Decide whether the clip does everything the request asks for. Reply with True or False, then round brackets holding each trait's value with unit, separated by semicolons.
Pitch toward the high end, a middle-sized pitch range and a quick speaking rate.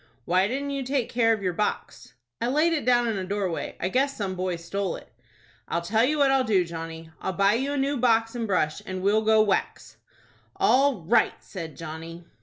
False (210 Hz; 5.7 semitones; 210 wpm)